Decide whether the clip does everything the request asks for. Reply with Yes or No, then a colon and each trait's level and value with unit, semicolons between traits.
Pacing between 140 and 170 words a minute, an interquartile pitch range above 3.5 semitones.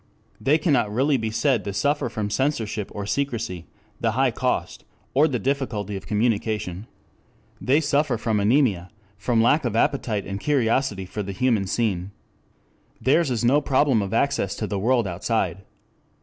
Yes: average, 160 wpm; average, 4.7 semitones